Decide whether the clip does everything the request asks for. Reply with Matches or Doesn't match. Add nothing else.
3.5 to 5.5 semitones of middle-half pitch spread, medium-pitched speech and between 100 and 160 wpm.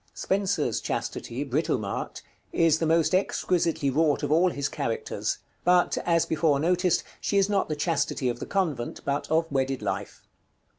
Matches